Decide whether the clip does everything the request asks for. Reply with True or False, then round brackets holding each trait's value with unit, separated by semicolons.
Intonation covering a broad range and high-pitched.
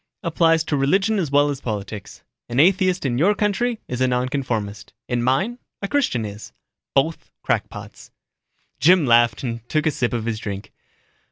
False (6.9 semitones; 135 Hz)